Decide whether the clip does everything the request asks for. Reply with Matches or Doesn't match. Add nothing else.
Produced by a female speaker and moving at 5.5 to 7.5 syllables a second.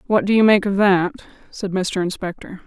Doesn't match